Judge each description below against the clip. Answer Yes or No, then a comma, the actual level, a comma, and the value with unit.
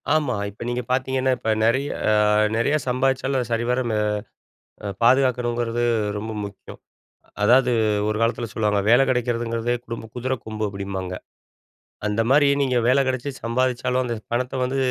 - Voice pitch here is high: No, low, 120 Hz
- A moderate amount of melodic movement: No, narrow, 2.1 semitones